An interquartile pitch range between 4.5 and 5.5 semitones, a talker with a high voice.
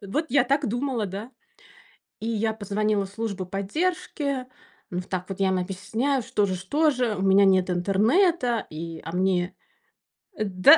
Yes: average, 5.2 semitones; high, 205 Hz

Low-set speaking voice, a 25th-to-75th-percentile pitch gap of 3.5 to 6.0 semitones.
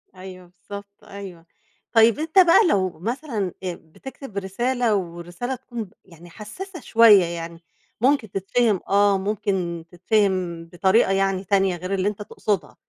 No: high, 195 Hz; average, 3.8 semitones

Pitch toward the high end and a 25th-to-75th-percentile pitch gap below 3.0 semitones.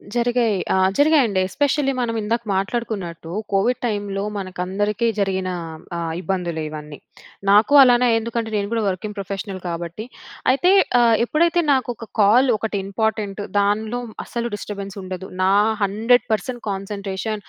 No: high, 210 Hz; average, 3.5 semitones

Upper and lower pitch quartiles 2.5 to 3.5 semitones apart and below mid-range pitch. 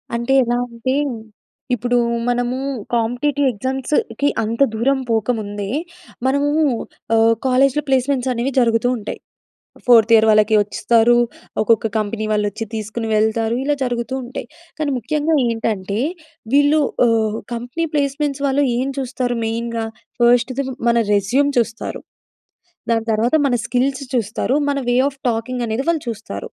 No: average, 3.0 semitones; high, 240 Hz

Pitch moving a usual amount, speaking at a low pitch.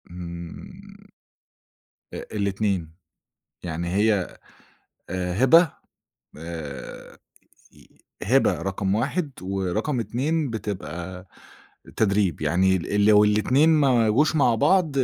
No: wide, 5.9 semitones; low, 100 Hz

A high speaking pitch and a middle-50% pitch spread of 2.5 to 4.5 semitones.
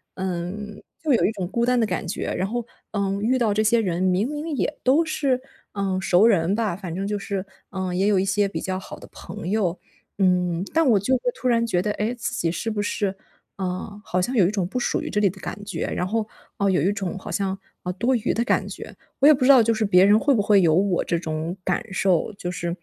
Yes: high, 200 Hz; average, 3.7 semitones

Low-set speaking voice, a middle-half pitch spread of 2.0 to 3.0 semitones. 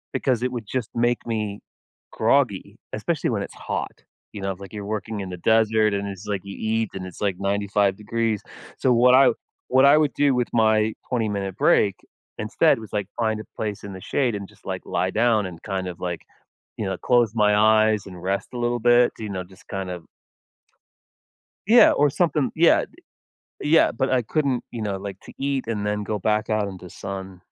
No: low, 110 Hz; average, 3.4 semitones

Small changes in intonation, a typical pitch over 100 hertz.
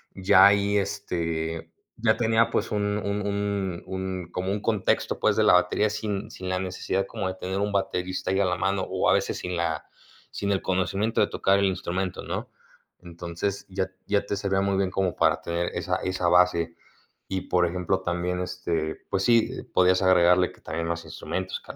No: narrow, 1.8 semitones; very low, 95 Hz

